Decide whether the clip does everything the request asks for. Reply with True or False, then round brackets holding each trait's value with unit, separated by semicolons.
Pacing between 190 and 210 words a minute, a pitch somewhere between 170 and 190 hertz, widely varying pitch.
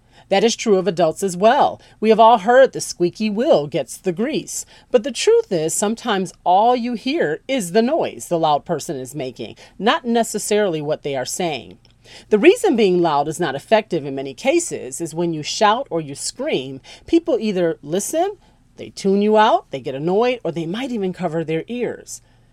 True (195 wpm; 185 Hz; 6.7 semitones)